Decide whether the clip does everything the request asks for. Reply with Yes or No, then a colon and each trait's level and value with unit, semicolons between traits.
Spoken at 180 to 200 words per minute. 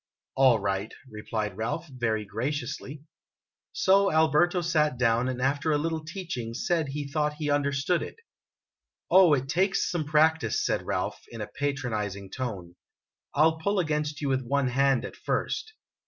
No: average, 160 wpm